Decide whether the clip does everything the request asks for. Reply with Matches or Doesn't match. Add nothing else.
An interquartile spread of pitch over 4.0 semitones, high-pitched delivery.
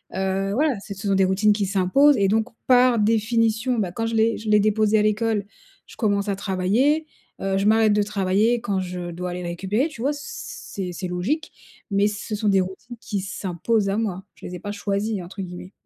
Doesn't match